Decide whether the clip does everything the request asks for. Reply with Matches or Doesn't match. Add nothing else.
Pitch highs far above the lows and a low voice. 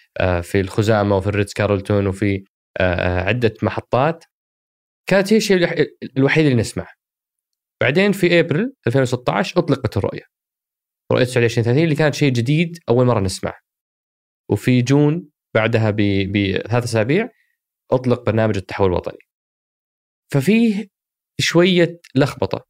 Matches